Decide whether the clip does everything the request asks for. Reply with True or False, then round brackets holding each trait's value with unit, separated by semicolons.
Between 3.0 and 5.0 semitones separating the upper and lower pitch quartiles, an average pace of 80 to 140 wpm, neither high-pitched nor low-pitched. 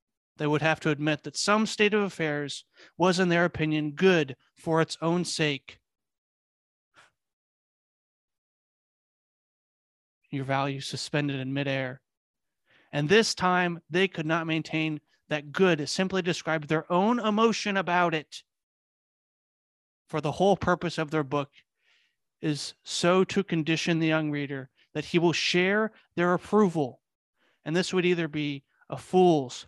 True (3.6 semitones; 135 wpm; 160 Hz)